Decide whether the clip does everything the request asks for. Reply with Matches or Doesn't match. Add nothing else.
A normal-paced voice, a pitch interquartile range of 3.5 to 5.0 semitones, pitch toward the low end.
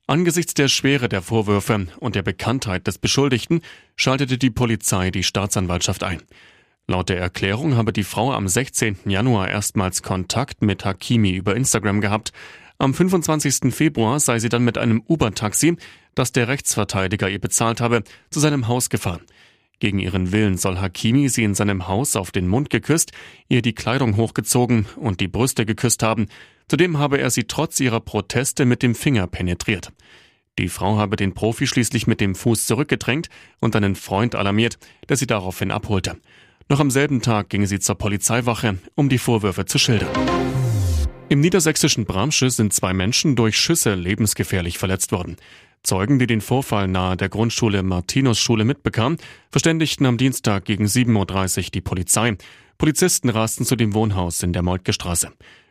Matches